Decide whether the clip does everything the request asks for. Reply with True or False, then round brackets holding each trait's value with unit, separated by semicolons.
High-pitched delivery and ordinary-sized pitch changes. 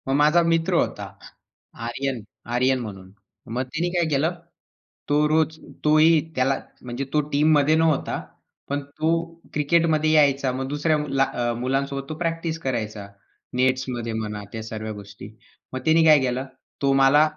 False (140 Hz; 3.4 semitones)